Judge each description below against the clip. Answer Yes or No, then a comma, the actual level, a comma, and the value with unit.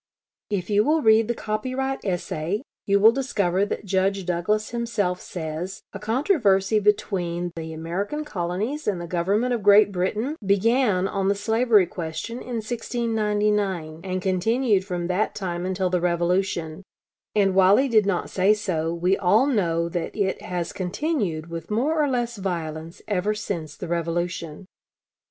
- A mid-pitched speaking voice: No, high, 195 Hz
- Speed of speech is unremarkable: Yes, average, 155 wpm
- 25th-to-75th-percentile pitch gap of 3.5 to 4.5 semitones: Yes, average, 3.8 semitones